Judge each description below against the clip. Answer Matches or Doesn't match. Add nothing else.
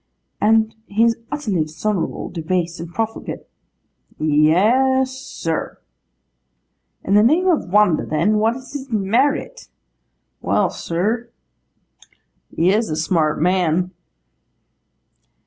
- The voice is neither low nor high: Doesn't match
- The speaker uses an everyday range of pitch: Doesn't match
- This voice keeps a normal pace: Doesn't match